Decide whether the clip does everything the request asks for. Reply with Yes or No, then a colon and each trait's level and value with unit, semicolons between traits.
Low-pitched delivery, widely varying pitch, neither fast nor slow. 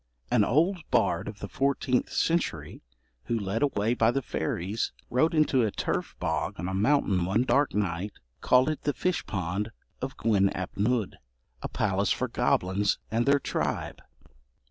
Yes: low, 110 Hz; wide, 5.7 semitones; average, 165 wpm